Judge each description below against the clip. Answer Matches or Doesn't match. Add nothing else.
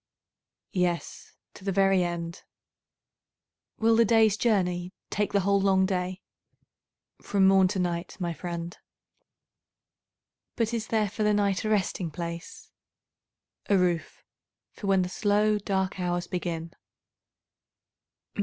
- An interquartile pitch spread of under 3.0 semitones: Matches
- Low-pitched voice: Doesn't match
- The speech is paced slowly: Matches